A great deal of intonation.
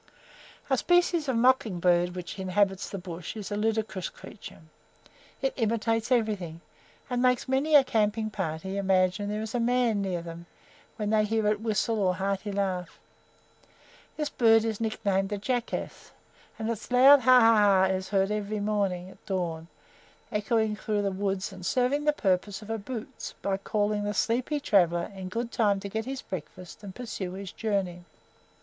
No: average, 3.2 semitones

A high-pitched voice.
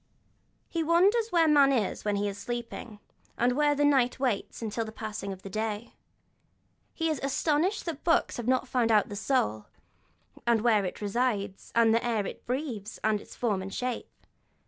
Yes: high, 235 Hz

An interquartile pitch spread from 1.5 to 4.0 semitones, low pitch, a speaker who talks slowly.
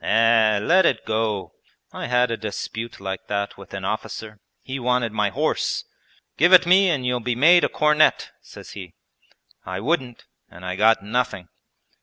No: average, 3.7 semitones; low, 115 Hz; average, 170 wpm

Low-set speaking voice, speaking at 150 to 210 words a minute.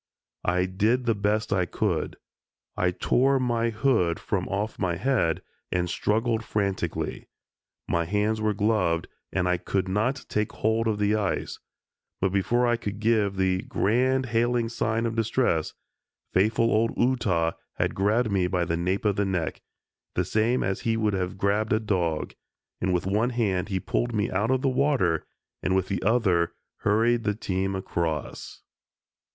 Yes: low, 105 Hz; average, 165 wpm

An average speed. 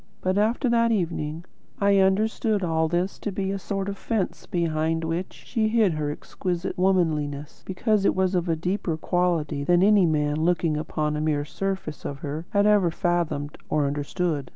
Yes: average, 175 wpm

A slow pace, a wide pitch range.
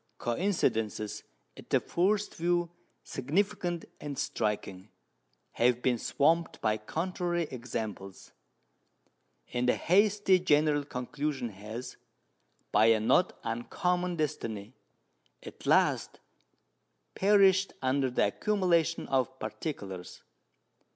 Yes: slow, 95 wpm; wide, 7.7 semitones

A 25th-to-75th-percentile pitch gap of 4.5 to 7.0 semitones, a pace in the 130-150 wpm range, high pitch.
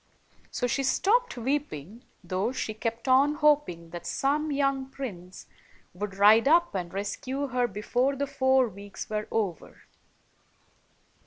Yes: wide, 5.5 semitones; average, 140 wpm; high, 245 Hz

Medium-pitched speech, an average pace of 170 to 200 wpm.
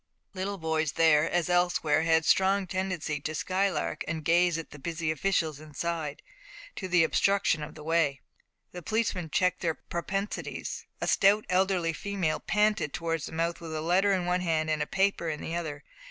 Yes: medium, 170 Hz; average, 185 wpm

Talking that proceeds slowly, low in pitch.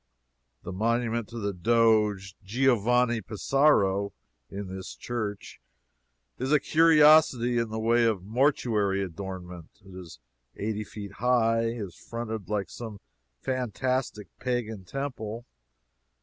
Yes: slow, 120 wpm; low, 110 Hz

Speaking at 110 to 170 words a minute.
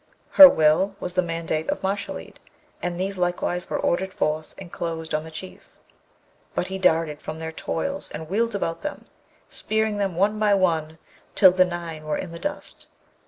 No: average, 180 wpm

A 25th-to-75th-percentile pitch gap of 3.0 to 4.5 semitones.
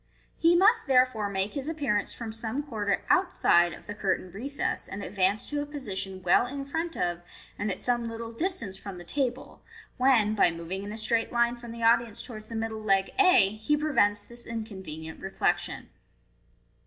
No: average, 5.0 semitones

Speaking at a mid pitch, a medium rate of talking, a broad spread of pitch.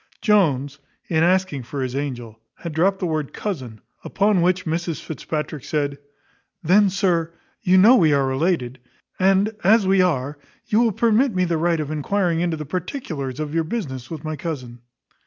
No: medium, 165 Hz; average, 175 wpm; average, 4.8 semitones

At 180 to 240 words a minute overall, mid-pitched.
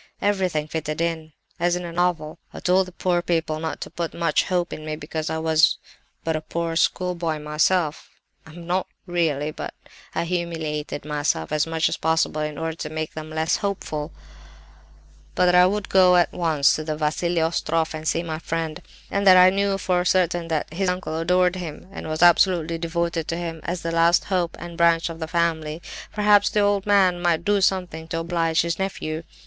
Yes: average, 200 wpm; medium, 165 Hz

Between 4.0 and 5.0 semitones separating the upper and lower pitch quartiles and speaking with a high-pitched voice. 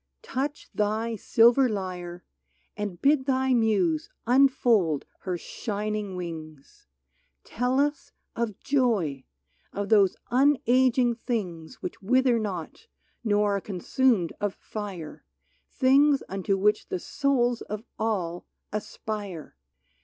No: wide, 5.4 semitones; high, 215 Hz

